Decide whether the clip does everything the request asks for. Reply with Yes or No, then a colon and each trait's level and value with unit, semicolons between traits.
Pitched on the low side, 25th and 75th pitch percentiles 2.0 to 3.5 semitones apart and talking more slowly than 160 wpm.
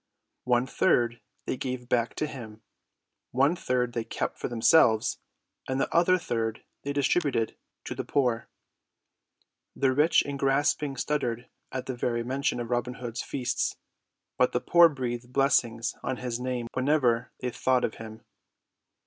Yes: low, 125 Hz; narrow, 2.6 semitones; average, 150 wpm